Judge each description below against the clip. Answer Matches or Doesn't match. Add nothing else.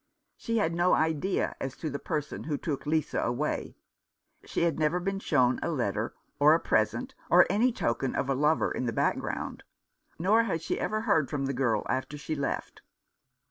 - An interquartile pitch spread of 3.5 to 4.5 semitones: Matches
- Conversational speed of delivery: Matches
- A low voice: Doesn't match